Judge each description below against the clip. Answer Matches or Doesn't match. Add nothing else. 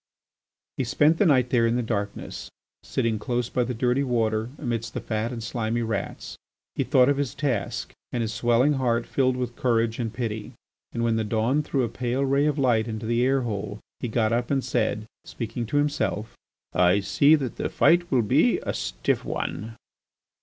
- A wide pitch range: Doesn't match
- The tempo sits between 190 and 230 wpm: Matches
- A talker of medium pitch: Doesn't match